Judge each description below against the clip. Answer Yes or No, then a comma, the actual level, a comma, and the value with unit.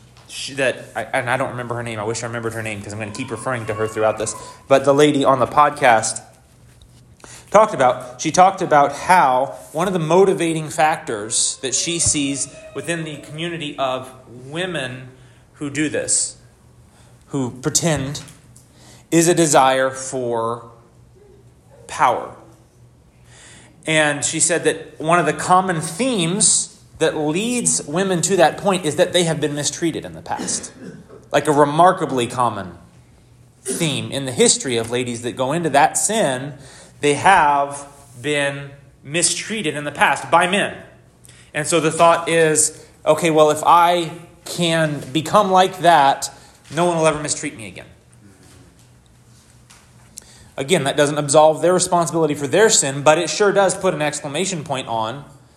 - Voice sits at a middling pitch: Yes, medium, 150 Hz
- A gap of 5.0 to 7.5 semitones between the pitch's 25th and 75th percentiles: No, average, 4.5 semitones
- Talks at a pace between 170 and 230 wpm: No, average, 160 wpm